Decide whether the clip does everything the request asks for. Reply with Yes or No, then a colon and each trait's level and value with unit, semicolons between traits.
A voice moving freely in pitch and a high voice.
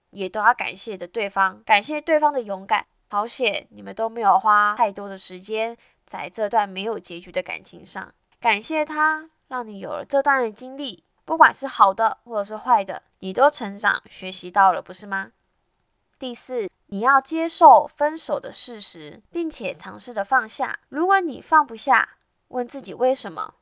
Yes: wide, 6.4 semitones; high, 235 Hz